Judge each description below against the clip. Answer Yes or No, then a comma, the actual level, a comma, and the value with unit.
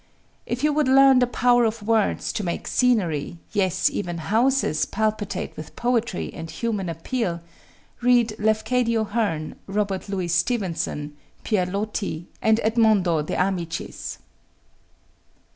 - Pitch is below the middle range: No, high, 210 Hz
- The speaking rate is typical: No, slow, 125 wpm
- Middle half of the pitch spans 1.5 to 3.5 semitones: No, average, 5.2 semitones